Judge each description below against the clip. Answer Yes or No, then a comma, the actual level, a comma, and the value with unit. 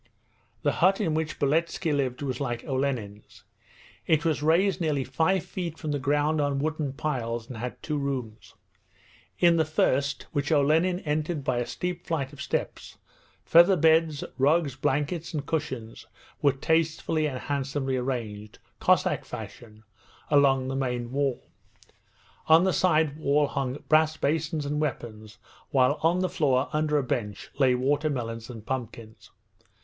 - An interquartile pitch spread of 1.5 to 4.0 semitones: Yes, average, 3.4 semitones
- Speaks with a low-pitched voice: No, medium, 145 Hz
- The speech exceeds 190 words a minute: No, average, 150 wpm